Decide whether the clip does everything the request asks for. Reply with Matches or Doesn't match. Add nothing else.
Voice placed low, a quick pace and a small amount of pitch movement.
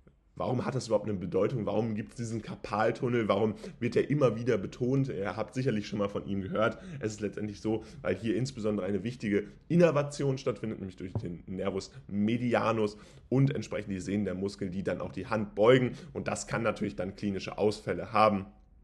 Doesn't match